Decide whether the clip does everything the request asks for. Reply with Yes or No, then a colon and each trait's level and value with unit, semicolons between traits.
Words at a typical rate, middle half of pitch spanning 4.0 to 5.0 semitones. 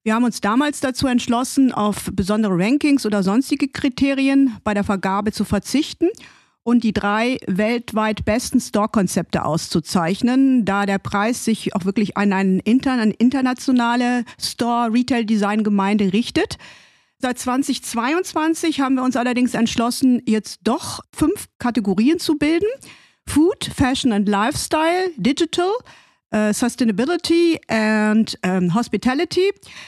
No: slow, 120 wpm; average, 4.3 semitones